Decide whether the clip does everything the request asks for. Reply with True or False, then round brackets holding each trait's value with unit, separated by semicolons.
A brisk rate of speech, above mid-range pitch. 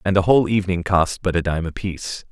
False (235 wpm; 90 Hz)